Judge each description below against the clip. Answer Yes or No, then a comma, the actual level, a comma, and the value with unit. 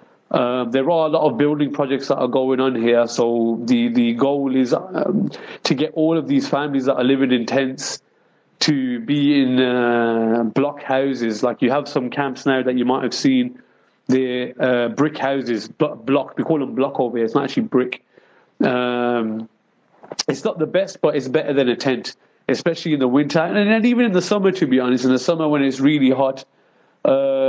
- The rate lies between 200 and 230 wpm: Yes, fast, 205 wpm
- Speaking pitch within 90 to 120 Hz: No, low, 135 Hz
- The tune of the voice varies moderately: Yes, average, 3.4 semitones